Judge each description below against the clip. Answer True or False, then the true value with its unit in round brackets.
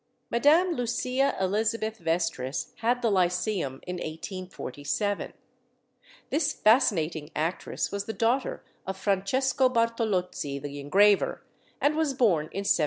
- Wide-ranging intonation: True (5.8 semitones)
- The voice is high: True (200 Hz)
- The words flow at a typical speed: False (115 wpm)